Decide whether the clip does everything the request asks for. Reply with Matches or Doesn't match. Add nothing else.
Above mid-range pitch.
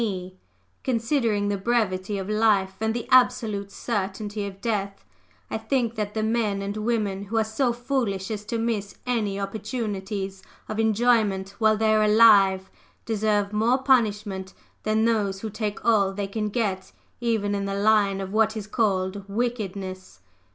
Matches